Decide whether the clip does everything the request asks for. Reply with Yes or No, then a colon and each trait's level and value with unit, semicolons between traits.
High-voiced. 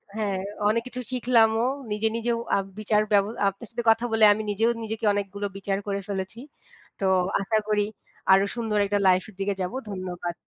Yes: high, 210 Hz